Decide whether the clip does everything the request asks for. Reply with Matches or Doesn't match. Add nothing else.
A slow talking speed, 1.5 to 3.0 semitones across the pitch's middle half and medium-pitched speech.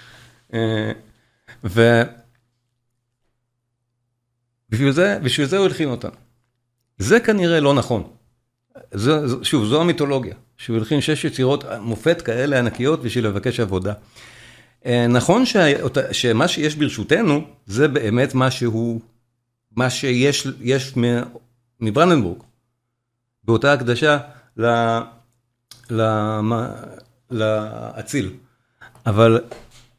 Doesn't match